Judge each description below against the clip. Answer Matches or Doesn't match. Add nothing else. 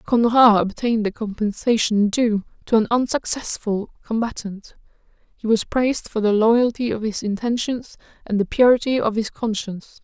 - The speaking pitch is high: Matches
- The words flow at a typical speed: Matches